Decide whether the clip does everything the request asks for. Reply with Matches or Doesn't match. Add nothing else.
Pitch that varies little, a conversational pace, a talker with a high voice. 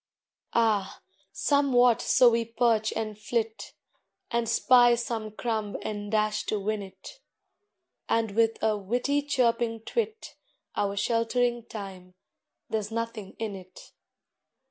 Doesn't match